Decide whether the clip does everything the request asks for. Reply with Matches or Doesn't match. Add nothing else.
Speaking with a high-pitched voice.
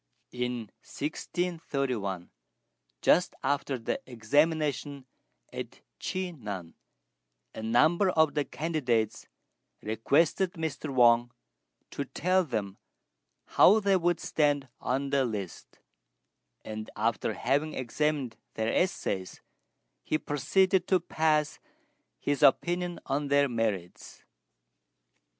Doesn't match